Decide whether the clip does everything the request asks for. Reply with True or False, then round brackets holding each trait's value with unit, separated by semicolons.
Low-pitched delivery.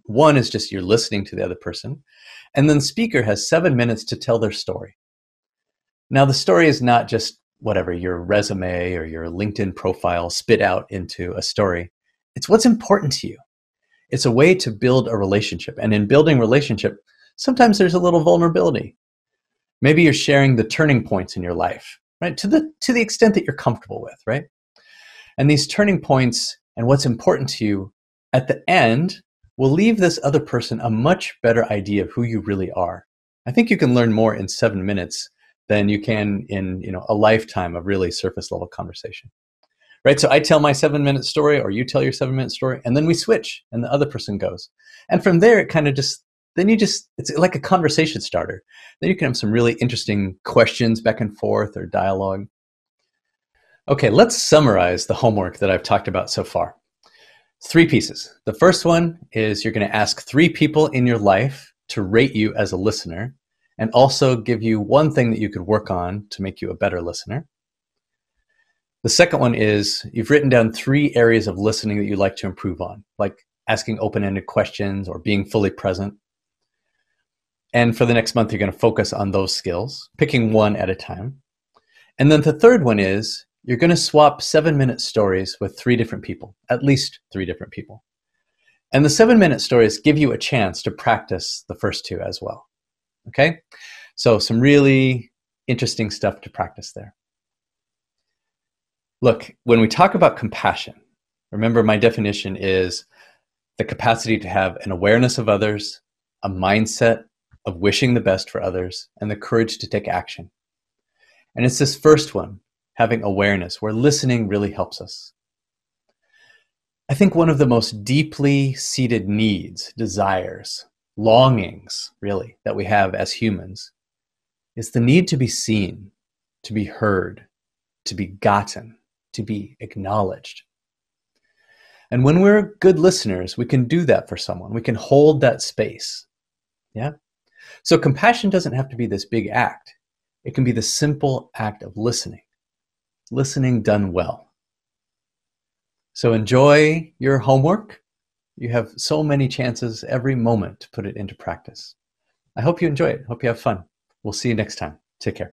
True (115 Hz)